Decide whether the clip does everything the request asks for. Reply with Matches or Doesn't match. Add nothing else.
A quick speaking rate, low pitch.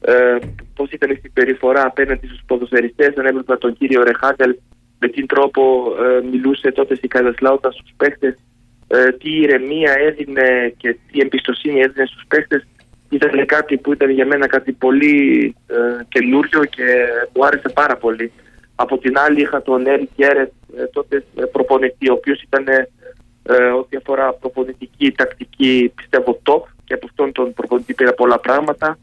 Doesn't match